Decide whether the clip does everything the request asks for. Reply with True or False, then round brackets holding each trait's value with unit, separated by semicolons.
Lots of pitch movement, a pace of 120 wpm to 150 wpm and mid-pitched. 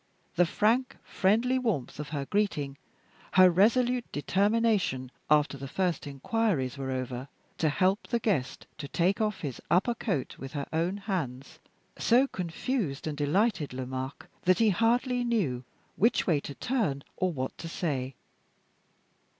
True (8.0 semitones; 145 wpm; 175 Hz)